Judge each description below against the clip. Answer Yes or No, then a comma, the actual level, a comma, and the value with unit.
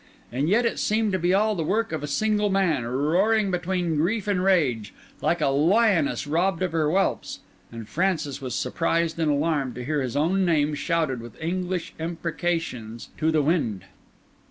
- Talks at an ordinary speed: Yes, average, 180 wpm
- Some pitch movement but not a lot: Yes, average, 4.6 semitones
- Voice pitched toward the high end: No, medium, 165 Hz